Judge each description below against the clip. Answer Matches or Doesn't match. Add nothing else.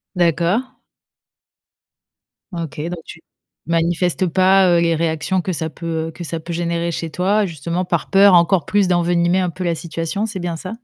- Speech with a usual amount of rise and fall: Doesn't match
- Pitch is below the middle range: Doesn't match